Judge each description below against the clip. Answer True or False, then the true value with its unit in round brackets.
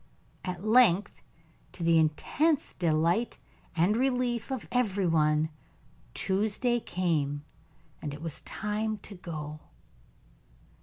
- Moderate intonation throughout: False (5.7 semitones)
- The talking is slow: True (110 wpm)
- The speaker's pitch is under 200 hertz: True (185 Hz)